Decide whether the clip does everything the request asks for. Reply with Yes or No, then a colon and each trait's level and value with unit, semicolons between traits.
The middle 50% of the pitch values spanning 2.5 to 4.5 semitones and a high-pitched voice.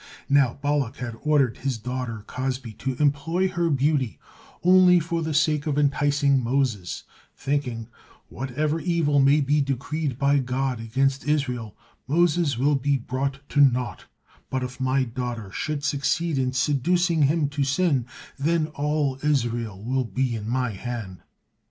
No: average, 3.0 semitones; medium, 140 Hz